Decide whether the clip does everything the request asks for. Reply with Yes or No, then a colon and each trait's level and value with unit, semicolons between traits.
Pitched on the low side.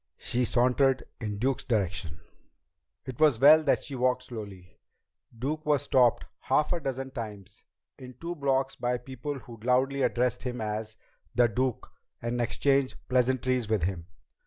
Yes: low, 125 Hz